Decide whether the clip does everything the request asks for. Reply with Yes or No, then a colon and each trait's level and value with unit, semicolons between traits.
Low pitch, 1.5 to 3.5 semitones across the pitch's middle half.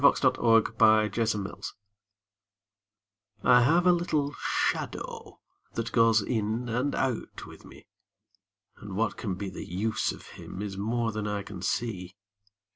Yes: low, 115 Hz; average, 3.1 semitones